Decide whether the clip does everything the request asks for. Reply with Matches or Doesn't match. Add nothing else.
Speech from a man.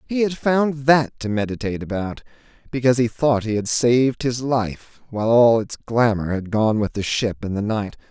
Matches